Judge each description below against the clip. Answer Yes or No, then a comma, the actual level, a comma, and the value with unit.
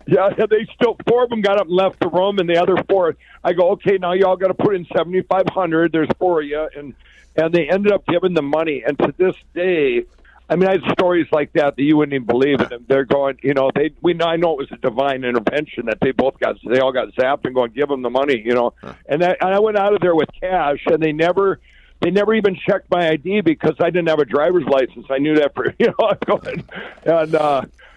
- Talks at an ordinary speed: No, fast, 270 wpm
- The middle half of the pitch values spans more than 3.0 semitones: Yes, average, 4.6 semitones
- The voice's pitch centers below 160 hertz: No, medium, 170 Hz